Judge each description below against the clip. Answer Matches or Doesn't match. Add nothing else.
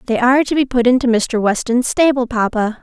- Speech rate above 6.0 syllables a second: Doesn't match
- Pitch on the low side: Doesn't match